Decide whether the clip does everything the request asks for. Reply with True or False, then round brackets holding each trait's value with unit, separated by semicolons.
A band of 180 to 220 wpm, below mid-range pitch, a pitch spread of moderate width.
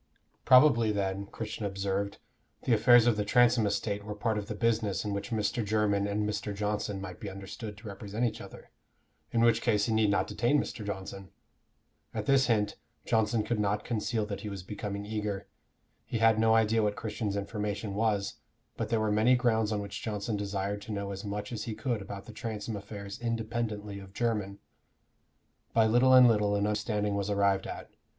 False (190 wpm; 105 Hz; 1.9 semitones)